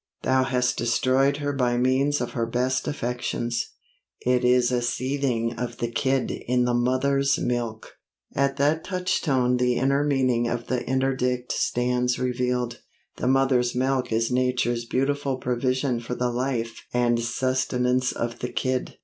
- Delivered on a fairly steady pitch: Yes, narrow, 1.5 semitones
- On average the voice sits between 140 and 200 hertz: No, low, 125 Hz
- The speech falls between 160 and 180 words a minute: No, average, 150 wpm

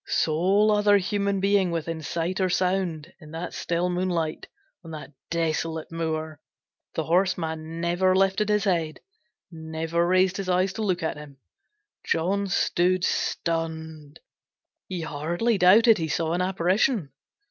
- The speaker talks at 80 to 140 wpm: Yes, slow, 135 wpm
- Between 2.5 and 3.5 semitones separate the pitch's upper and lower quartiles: Yes, average, 2.8 semitones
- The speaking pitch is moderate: Yes, medium, 175 Hz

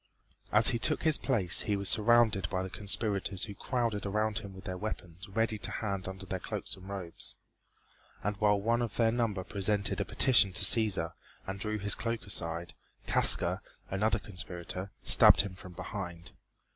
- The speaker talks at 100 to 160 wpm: No, average, 175 wpm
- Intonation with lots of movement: No, average, 2.7 semitones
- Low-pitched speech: Yes, low, 100 Hz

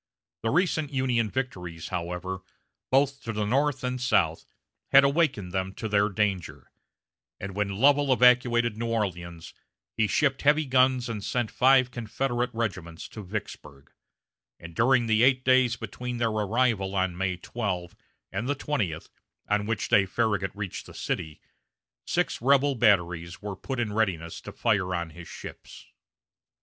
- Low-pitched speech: Yes, low, 110 Hz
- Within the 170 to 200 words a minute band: No, average, 150 wpm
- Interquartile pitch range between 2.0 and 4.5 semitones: No, average, 5.2 semitones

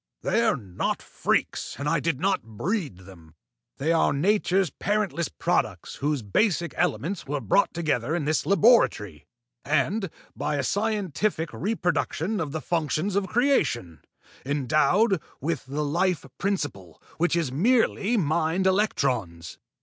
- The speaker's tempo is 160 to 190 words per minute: No, slow, 135 wpm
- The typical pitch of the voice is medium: Yes, medium, 160 Hz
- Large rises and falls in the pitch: Yes, wide, 6.2 semitones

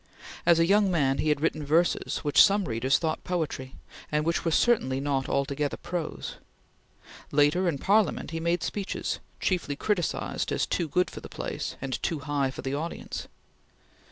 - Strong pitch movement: No, average, 3.9 semitones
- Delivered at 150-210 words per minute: Yes, average, 170 wpm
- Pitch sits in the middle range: Yes, medium, 155 Hz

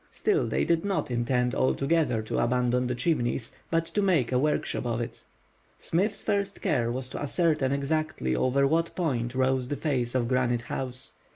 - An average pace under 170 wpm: No, average, 175 wpm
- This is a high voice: No, low, 130 Hz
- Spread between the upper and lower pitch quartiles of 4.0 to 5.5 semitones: Yes, average, 4.7 semitones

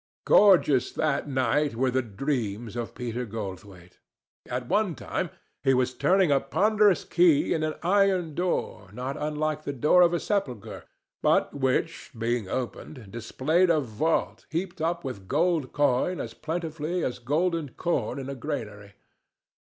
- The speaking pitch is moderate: Yes, medium, 145 Hz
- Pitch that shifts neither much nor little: No, wide, 5.7 semitones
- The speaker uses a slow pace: No, average, 150 wpm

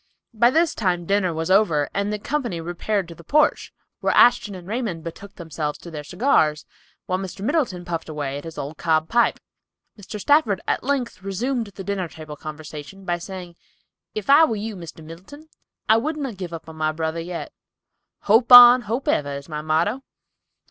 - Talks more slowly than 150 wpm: No, average, 185 wpm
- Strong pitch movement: Yes, wide, 5.7 semitones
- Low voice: No, medium, 185 Hz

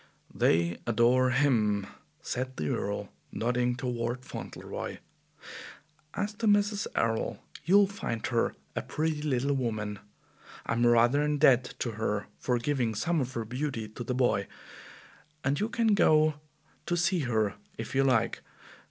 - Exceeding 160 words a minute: No, average, 145 wpm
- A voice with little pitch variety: No, average, 4.5 semitones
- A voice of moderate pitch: No, low, 125 Hz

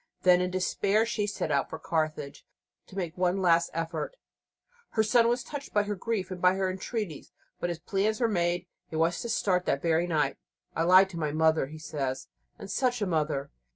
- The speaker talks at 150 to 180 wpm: No, average, 200 wpm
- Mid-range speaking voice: Yes, medium, 180 Hz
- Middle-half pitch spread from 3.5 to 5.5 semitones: Yes, average, 4.2 semitones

